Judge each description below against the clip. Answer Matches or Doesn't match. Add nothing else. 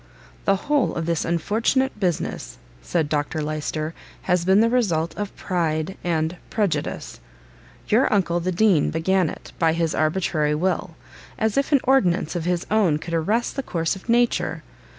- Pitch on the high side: Doesn't match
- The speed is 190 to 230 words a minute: Doesn't match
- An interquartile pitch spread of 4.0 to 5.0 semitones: Matches